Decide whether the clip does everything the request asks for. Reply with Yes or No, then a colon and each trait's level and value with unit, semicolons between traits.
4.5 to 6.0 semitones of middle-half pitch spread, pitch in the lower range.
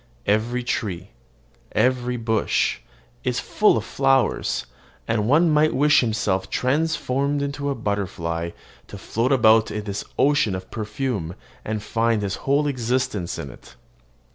Yes: average, 4.8 semitones; low, 115 Hz